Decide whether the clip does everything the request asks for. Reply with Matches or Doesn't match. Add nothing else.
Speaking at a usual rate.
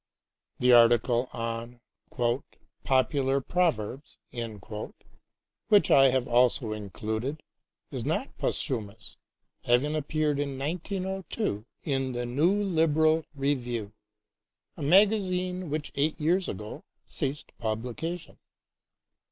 Doesn't match